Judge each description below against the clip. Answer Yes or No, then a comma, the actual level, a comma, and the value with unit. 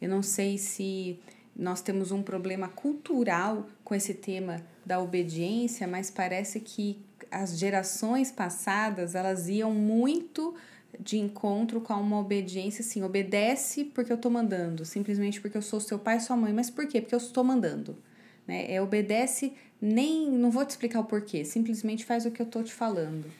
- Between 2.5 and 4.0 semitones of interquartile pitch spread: Yes, average, 3.5 semitones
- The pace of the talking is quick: No, average, 175 wpm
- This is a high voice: Yes, high, 210 Hz